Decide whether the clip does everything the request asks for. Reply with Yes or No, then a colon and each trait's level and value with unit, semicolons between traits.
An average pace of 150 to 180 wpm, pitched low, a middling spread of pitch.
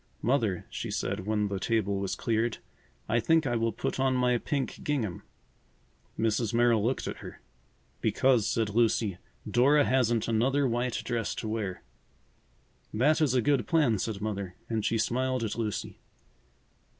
Yes: average, 155 wpm; low, 115 Hz; average, 3.1 semitones